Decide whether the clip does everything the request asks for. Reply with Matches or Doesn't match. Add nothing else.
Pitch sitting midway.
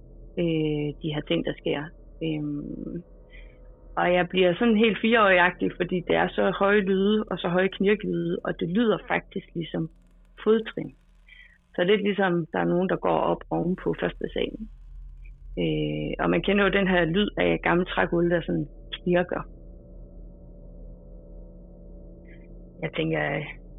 Matches